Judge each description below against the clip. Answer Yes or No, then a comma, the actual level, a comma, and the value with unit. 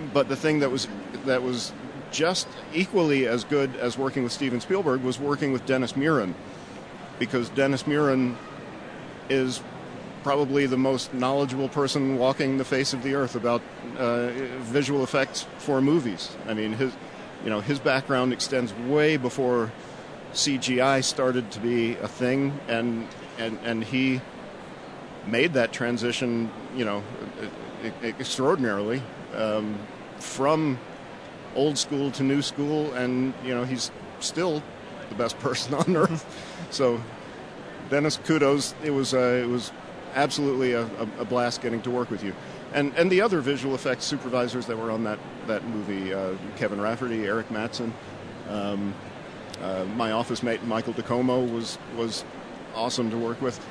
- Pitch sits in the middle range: No, low, 125 Hz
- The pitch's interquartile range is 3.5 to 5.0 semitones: No, average, 2.9 semitones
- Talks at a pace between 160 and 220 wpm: No, average, 150 wpm